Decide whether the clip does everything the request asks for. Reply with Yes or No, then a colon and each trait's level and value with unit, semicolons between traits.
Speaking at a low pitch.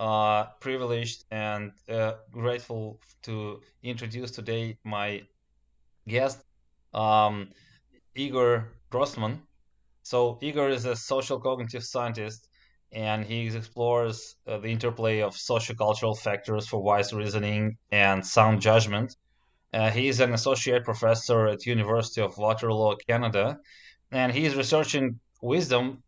Yes: low, 115 Hz